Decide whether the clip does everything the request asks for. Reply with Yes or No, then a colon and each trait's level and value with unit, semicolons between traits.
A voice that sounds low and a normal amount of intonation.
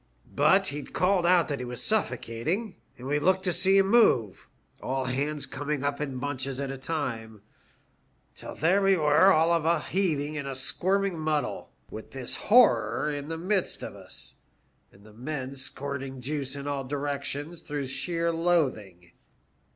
No: medium, 145 Hz; average, 4.4 semitones